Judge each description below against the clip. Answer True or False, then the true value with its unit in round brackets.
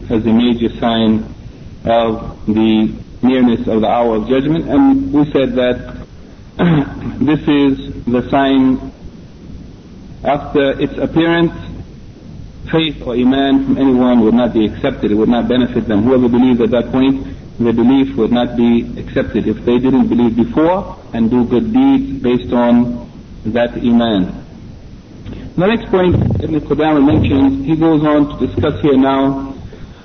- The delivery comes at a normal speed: True (150 wpm)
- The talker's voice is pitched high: False (125 Hz)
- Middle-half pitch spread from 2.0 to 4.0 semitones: True (3.2 semitones)